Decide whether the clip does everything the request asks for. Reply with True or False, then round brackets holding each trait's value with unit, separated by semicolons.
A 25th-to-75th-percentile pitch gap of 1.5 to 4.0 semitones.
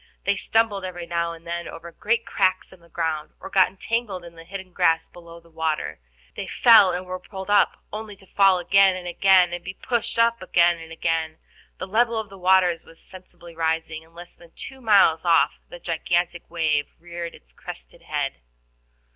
True (2.7 semitones)